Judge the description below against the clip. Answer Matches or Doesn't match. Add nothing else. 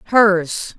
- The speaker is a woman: Matches